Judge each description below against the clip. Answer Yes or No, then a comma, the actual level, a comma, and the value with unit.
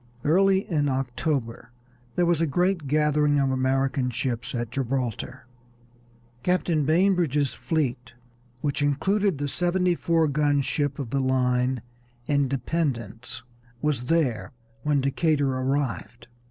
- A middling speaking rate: No, slow, 115 wpm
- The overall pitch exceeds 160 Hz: No, medium, 140 Hz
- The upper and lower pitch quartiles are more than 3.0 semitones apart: Yes, average, 3.6 semitones